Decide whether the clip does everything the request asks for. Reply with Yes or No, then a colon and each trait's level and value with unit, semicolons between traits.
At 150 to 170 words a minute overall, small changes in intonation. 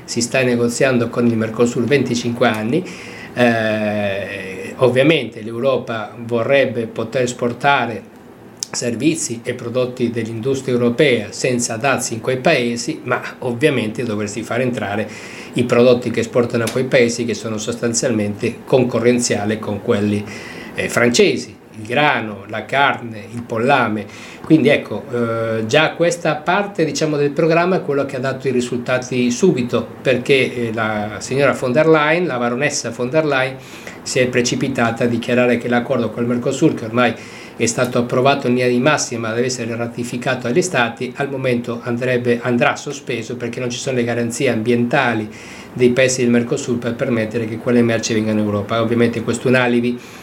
Yes: average, 155 wpm; narrow, 1.9 semitones